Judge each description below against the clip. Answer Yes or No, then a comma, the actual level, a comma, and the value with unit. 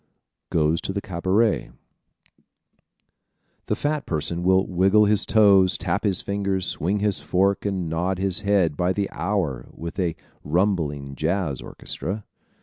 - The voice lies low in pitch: Yes, very low, 95 Hz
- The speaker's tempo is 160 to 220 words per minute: No, average, 145 wpm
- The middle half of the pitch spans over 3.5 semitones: No, average, 3.1 semitones